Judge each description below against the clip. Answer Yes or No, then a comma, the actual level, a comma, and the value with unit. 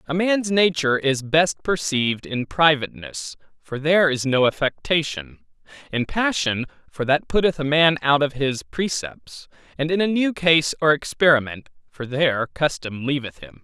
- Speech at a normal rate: Yes, average, 160 wpm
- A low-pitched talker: No, medium, 145 Hz